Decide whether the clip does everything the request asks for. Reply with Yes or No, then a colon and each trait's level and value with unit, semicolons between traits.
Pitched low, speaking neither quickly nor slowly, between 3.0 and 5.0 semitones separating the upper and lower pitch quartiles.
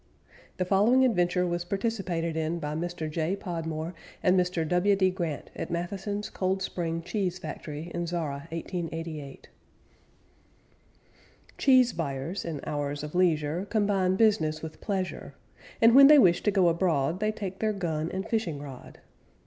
No: medium, 175 Hz; average, 150 wpm; average, 3.4 semitones